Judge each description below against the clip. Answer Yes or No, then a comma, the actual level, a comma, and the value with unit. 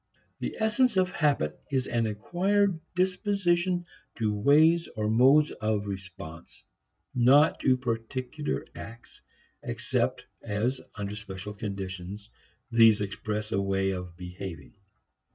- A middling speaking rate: No, slow, 115 wpm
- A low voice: Yes, low, 115 Hz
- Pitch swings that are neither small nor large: No, wide, 7.5 semitones